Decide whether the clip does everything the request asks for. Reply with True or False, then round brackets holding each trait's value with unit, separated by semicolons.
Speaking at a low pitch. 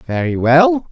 True (125 Hz)